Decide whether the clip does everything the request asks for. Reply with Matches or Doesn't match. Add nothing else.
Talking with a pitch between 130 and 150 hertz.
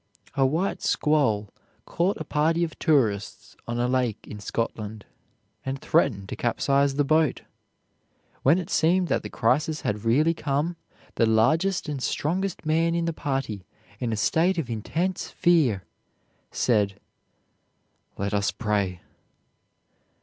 Matches